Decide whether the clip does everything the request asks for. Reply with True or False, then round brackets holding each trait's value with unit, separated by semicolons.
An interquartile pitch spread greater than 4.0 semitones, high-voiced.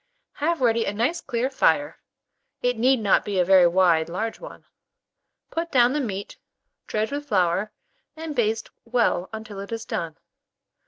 True (5.0 semitones; 225 Hz)